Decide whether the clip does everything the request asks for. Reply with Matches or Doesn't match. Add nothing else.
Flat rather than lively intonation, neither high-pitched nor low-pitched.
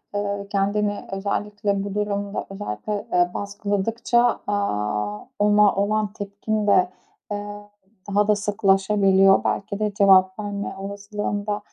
Doesn't match